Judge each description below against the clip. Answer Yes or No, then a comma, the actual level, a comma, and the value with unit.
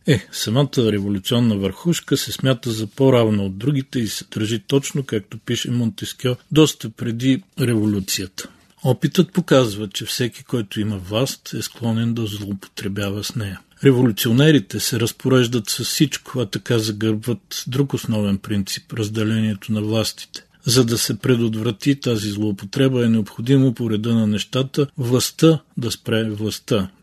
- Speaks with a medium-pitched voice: No, low, 115 Hz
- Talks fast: No, average, 140 wpm